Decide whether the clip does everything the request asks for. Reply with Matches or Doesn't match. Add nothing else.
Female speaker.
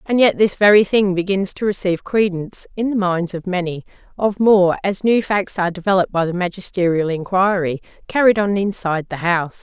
Matches